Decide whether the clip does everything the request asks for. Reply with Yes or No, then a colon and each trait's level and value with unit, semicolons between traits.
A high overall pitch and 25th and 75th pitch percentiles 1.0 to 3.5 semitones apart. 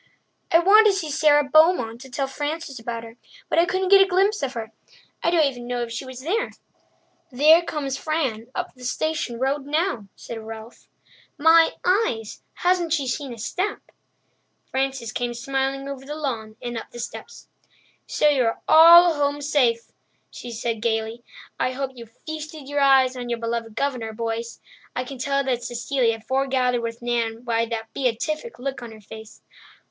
No: very high, 265 Hz; average, 4.6 semitones